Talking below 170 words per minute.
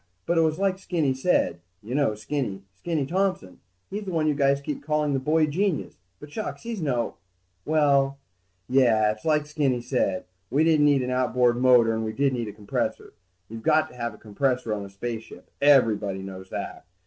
No: average, 195 wpm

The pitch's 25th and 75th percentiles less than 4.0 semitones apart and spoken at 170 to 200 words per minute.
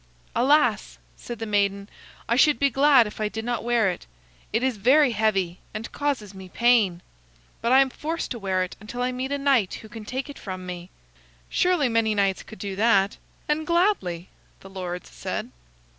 No: average, 5.3 semitones; average, 190 wpm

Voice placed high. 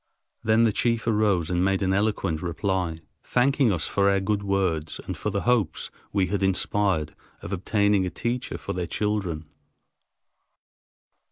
No: low, 100 Hz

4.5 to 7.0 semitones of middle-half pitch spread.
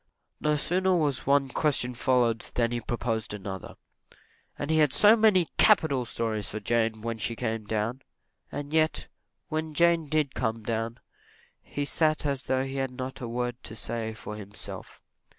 Yes: average, 5.0 semitones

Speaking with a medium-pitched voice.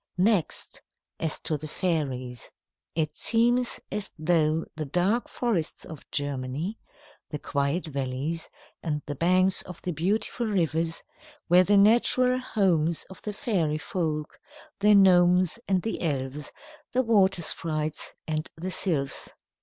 Yes: medium, 170 Hz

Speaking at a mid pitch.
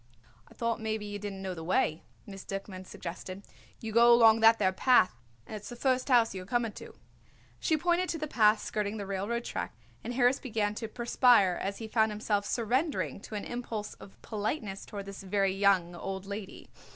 No: high, 210 Hz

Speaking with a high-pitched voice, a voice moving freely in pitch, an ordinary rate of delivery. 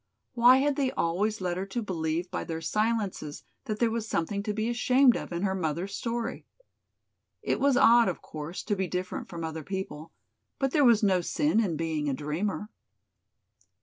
Yes: high, 195 Hz; wide, 5.7 semitones; average, 185 wpm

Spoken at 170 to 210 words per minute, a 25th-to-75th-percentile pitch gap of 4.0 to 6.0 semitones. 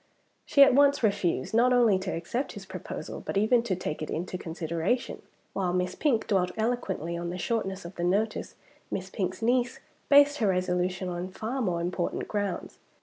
Yes: average, 180 wpm; average, 4.7 semitones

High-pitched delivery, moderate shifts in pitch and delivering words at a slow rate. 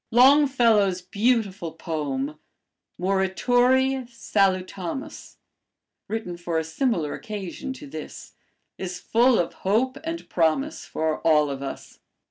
No: high, 195 Hz; wide, 6.8 semitones; slow, 105 wpm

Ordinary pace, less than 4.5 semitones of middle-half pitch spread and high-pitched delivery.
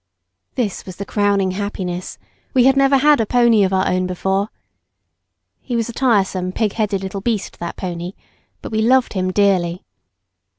Yes: average, 165 wpm; average, 4.0 semitones; high, 200 Hz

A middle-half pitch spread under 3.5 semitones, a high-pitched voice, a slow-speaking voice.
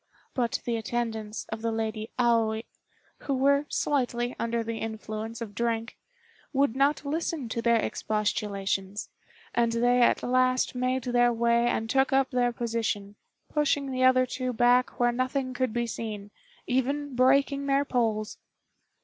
No: narrow, 2.4 semitones; high, 240 Hz; average, 150 wpm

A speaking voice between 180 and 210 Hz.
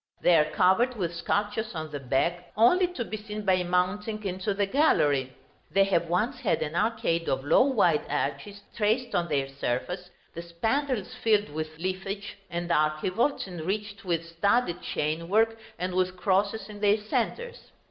Yes: medium, 185 Hz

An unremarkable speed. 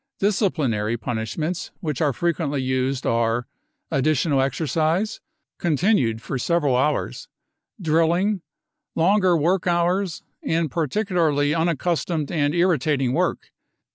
No: slow, 105 wpm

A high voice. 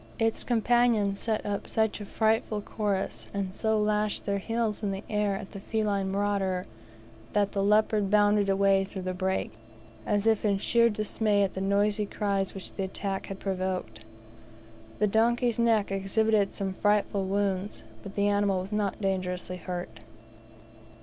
Yes: high, 200 Hz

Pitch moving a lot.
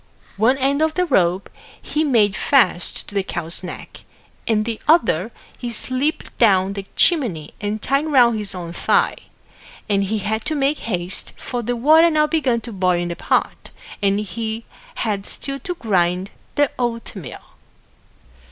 Yes: wide, 6.1 semitones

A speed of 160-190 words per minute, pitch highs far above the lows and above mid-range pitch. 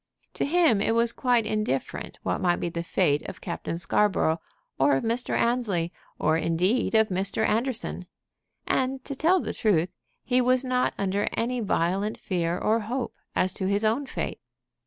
Yes: average, 170 wpm; wide, 5.8 semitones; high, 215 Hz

